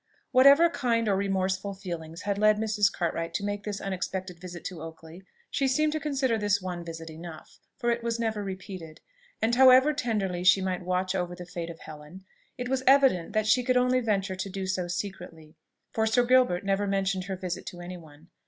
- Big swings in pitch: No, average, 4.4 semitones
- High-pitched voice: Yes, high, 195 Hz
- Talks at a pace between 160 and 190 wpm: No, average, 200 wpm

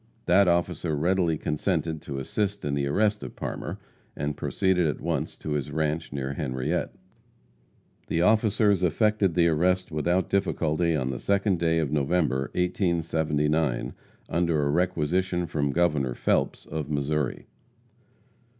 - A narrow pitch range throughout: No, average, 3.5 semitones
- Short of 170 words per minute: Yes, slow, 135 wpm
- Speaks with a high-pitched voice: No, very low, 80 Hz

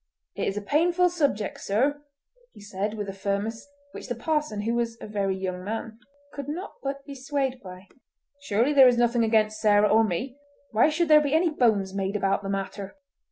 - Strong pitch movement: Yes, wide, 5.7 semitones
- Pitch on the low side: No, high, 225 Hz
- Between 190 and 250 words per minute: Yes, average, 200 wpm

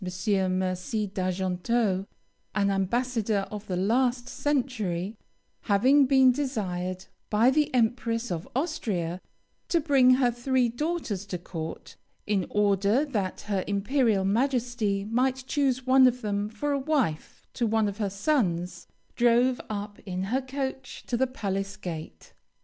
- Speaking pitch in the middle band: No, high, 220 Hz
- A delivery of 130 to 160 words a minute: Yes, slow, 135 wpm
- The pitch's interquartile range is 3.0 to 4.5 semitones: No, average, 5.0 semitones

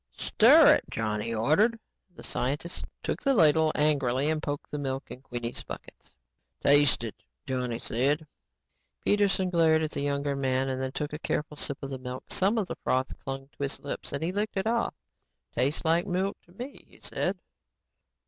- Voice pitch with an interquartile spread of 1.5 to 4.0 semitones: No, average, 4.4 semitones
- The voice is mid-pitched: Yes, medium, 145 Hz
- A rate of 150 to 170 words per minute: No, average, 185 wpm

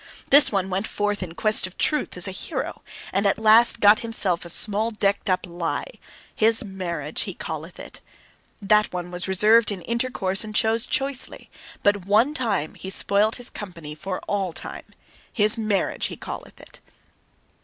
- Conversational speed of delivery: Yes, average, 175 wpm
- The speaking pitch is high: Yes, high, 205 Hz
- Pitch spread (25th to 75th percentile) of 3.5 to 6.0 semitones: No, average, 3.0 semitones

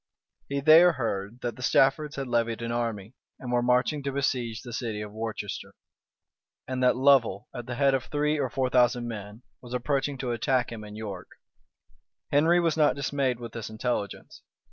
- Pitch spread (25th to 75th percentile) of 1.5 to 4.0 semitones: Yes, average, 3.1 semitones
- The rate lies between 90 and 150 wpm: No, average, 185 wpm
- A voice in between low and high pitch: No, low, 125 Hz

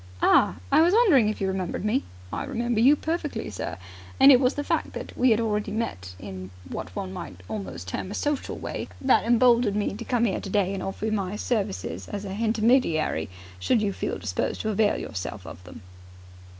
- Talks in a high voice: Yes, high, 210 Hz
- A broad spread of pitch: Yes, wide, 7.3 semitones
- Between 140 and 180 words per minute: No, fast, 205 wpm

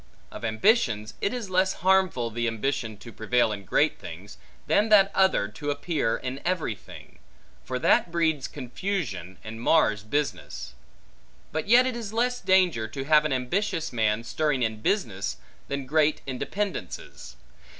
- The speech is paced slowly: No, average, 155 wpm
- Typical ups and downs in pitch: No, wide, 8.7 semitones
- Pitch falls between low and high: Yes, medium, 145 Hz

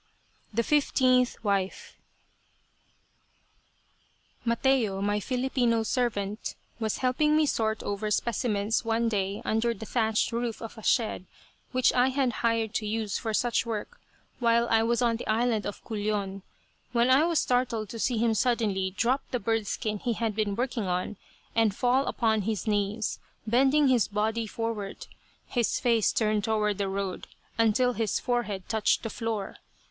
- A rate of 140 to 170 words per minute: Yes, average, 155 wpm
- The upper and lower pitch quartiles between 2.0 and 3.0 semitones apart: Yes, narrow, 2.6 semitones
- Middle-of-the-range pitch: No, high, 225 Hz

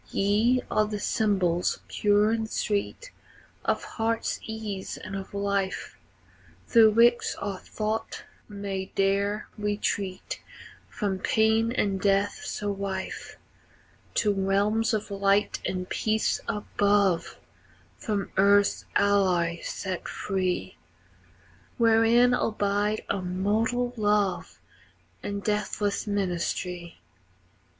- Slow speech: Yes, slow, 95 wpm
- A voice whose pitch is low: No, high, 205 Hz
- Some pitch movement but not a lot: No, narrow, 1.8 semitones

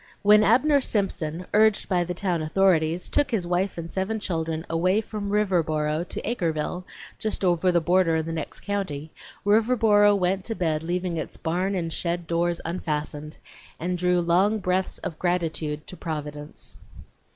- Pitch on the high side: No, medium, 180 Hz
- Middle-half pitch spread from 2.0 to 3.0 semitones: No, average, 3.6 semitones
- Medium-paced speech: Yes, average, 160 wpm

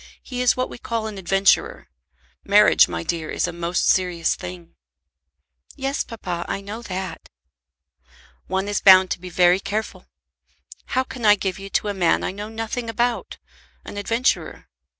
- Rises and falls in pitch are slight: No, average, 3.9 semitones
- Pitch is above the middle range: Yes, high, 195 Hz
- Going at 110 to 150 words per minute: No, average, 165 wpm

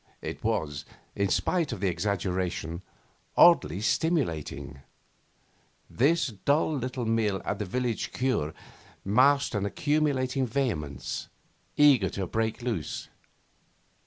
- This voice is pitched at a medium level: No, low, 110 Hz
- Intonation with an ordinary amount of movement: No, wide, 6.6 semitones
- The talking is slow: Yes, slow, 105 wpm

